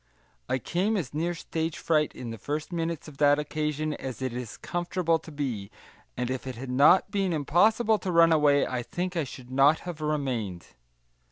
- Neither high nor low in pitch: Yes, medium, 150 Hz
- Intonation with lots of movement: No, average, 4.4 semitones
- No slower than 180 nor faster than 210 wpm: Yes, average, 190 wpm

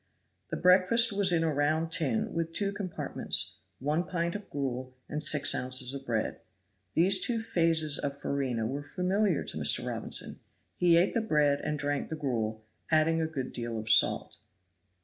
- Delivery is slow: No, average, 170 wpm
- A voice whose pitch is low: No, medium, 155 Hz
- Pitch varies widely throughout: No, average, 4.6 semitones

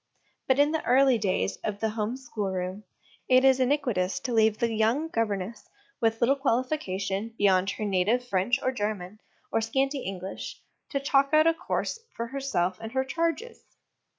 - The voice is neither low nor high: No, high, 230 Hz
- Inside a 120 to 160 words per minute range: No, average, 170 wpm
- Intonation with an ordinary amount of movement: Yes, average, 5.0 semitones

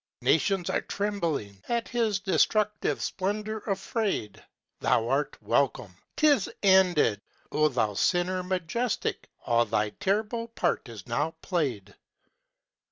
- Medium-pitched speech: Yes, medium, 180 Hz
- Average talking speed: No, slow, 110 wpm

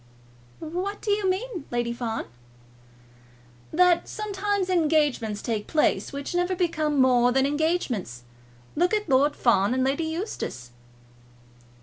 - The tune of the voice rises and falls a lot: Yes, wide, 6.5 semitones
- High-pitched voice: Yes, very high, 310 Hz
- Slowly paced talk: Yes, slow, 120 wpm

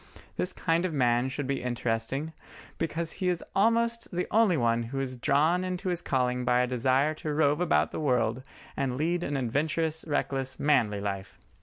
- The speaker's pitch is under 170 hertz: Yes, medium, 140 Hz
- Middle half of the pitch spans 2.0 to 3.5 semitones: No, average, 4.9 semitones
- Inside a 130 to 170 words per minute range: No, average, 180 wpm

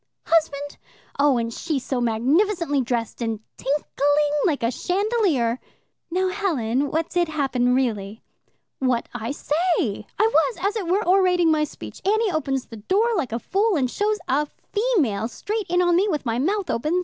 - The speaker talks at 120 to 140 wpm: No, average, 170 wpm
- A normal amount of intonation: No, wide, 7.1 semitones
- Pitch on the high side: Yes, very high, 300 Hz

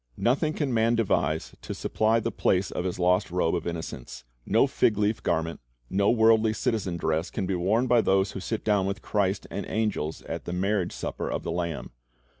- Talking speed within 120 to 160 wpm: No, average, 200 wpm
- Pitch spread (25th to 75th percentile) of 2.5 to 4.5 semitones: Yes, average, 3.9 semitones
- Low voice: Yes, low, 100 Hz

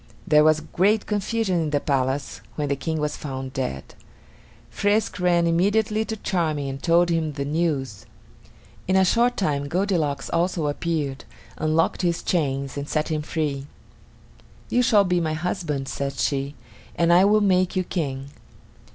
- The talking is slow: No, average, 160 wpm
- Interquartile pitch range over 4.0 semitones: Yes, average, 4.5 semitones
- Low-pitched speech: No, medium, 160 Hz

